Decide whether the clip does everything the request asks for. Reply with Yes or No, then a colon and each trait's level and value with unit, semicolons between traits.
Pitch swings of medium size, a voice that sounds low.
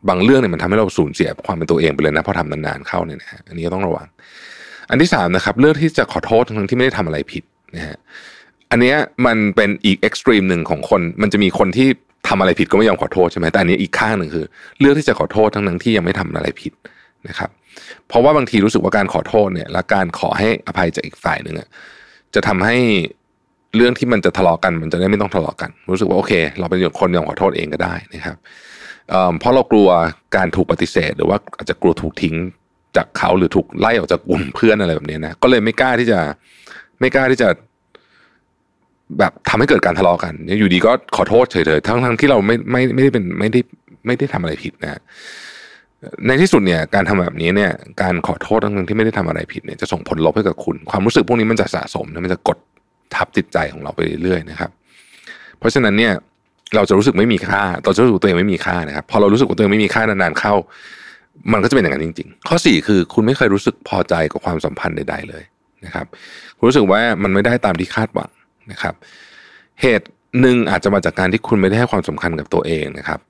No: wide, 5.7 semitones; low, 100 Hz